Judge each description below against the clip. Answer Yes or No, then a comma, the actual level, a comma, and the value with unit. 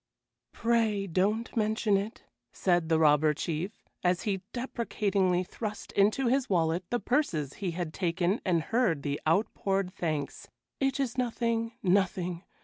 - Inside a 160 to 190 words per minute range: No, average, 140 wpm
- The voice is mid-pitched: No, high, 195 Hz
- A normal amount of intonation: Yes, average, 4.9 semitones